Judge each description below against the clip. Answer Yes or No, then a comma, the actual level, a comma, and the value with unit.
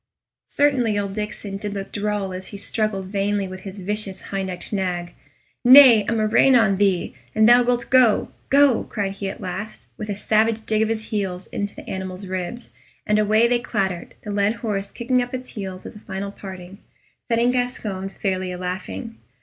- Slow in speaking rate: No, average, 185 wpm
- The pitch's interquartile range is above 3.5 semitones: No, average, 2.8 semitones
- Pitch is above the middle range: Yes, high, 205 Hz